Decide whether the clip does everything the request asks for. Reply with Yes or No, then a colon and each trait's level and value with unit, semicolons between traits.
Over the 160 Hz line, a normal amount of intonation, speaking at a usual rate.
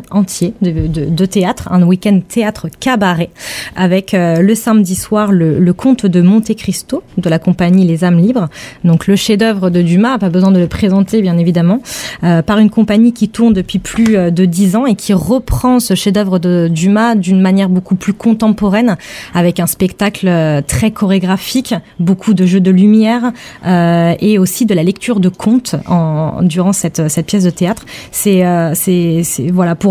Yes: high, 190 Hz; average, 3.2 semitones; average, 185 wpm